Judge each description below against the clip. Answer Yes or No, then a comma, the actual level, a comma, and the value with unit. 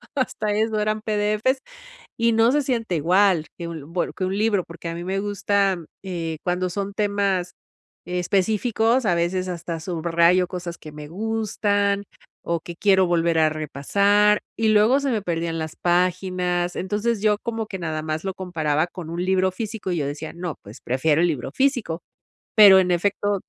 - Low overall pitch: No, medium, 185 Hz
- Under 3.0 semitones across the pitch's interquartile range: No, average, 3.6 semitones